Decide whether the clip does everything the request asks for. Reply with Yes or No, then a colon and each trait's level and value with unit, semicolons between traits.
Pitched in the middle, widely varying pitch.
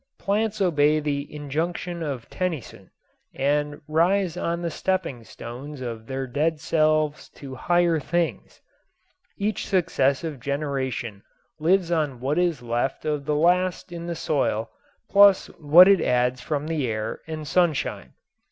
No: medium, 155 Hz; average, 4.1 semitones